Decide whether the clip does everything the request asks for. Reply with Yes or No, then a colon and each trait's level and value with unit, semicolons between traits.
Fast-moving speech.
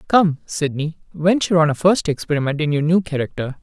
No: average, 180 wpm